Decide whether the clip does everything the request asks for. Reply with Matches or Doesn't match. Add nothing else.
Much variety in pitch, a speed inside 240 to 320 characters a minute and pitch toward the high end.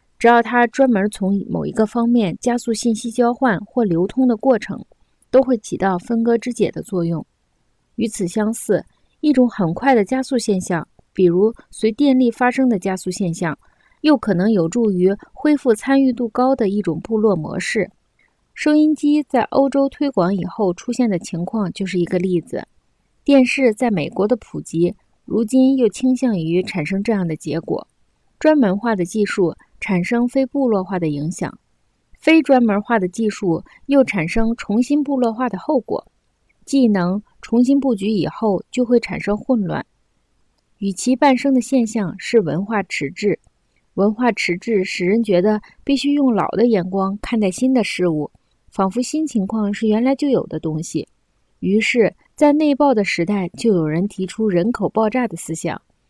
Doesn't match